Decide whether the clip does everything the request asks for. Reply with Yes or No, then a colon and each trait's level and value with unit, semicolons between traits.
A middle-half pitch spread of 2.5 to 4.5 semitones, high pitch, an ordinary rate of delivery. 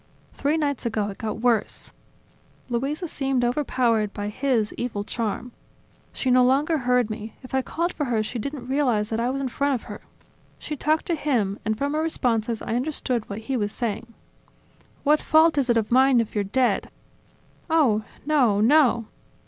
Yes: average, 4.2 semitones; high, 245 Hz; average, 180 wpm